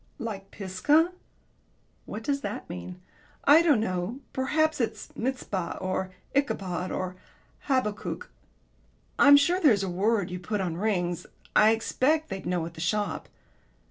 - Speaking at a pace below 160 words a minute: Yes, average, 140 wpm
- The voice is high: Yes, high, 210 Hz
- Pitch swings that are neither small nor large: No, wide, 6.8 semitones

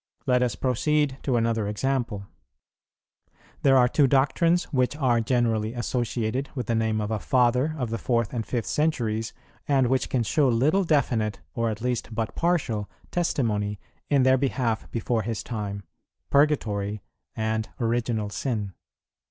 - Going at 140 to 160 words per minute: Yes, average, 150 wpm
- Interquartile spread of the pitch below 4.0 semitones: Yes, average, 3.2 semitones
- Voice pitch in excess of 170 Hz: No, low, 120 Hz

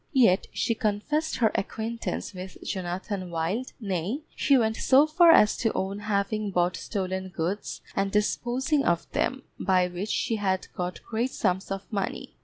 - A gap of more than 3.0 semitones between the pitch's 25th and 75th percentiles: Yes, average, 3.8 semitones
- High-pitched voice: Yes, high, 205 Hz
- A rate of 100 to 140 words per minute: No, average, 160 wpm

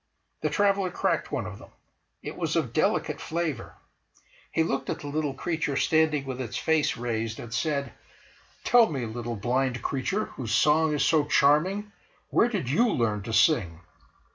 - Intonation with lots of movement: No, average, 5.0 semitones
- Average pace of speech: Yes, average, 165 wpm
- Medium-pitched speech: Yes, medium, 145 Hz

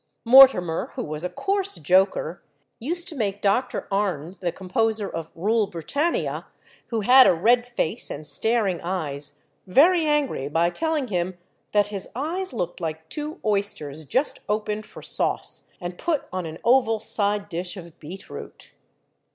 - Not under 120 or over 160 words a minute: Yes, average, 150 wpm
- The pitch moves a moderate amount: No, wide, 6.2 semitones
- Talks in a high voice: Yes, high, 205 Hz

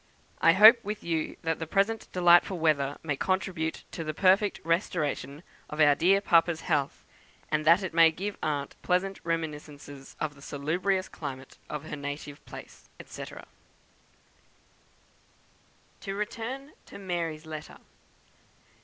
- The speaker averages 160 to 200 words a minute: No, slow, 135 wpm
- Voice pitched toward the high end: No, medium, 165 Hz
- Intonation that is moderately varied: Yes, average, 4.0 semitones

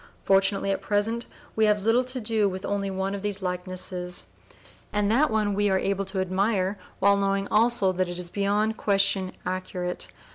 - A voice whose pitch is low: No, high, 200 Hz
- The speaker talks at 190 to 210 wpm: No, average, 175 wpm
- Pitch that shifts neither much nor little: No, narrow, 1.9 semitones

